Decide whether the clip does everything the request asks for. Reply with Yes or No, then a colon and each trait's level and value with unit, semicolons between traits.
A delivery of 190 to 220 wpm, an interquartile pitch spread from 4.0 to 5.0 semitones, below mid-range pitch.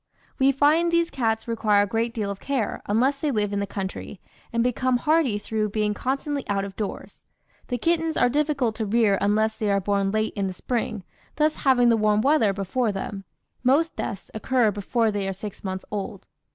No: average, 200 wpm; average, 4.3 semitones; high, 220 Hz